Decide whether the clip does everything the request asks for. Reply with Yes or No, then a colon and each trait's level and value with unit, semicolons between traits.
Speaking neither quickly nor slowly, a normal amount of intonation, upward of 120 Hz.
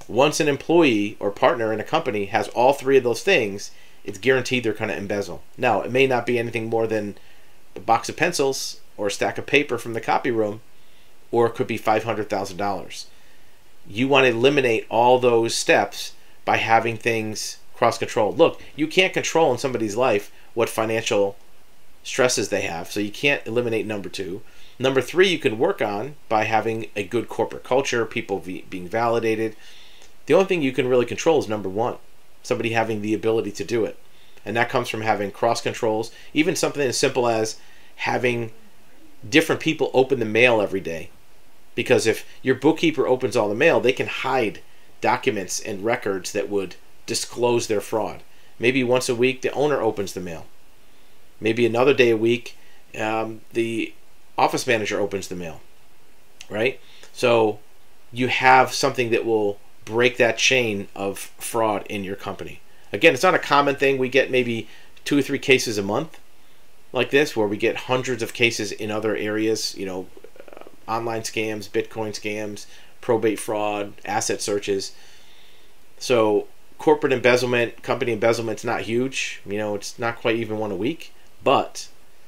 No: average, 170 wpm; average, 3.2 semitones; low, 115 Hz